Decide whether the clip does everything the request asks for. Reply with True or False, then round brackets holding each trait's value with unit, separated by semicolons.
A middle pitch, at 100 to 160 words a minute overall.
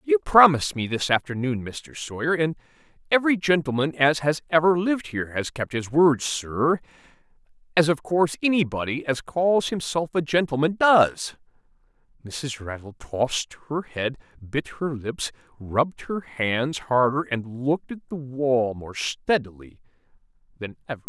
True (145 Hz; 145 wpm)